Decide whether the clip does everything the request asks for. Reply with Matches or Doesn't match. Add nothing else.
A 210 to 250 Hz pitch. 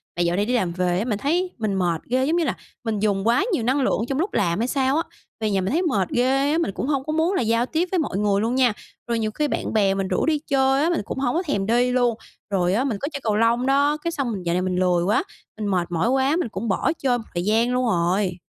Matches